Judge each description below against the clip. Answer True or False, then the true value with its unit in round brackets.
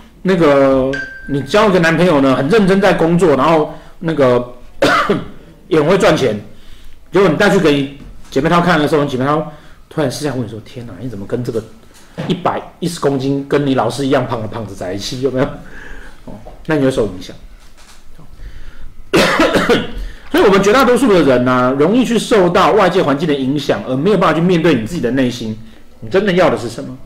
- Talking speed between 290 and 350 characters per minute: True (295 characters per minute)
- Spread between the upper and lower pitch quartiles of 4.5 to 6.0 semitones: True (5.4 semitones)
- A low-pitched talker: False (145 Hz)